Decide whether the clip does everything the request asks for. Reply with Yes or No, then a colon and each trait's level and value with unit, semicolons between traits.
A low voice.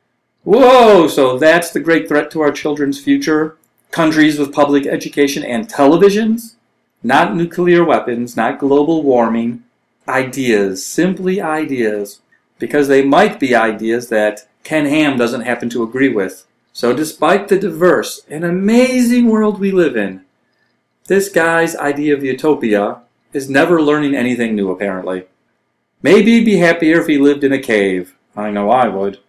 No: medium, 145 Hz